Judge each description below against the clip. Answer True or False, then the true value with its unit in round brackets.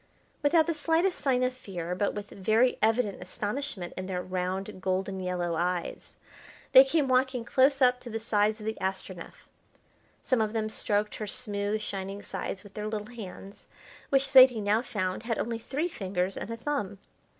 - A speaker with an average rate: True (175 wpm)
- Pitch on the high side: True (215 Hz)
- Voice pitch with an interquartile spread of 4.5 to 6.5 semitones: True (4.9 semitones)